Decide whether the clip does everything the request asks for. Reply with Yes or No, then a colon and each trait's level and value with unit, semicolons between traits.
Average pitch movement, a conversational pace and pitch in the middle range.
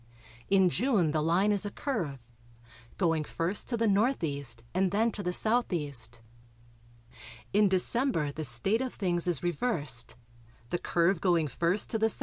Yes: average, 4.7 semitones; average, 155 wpm; medium, 180 Hz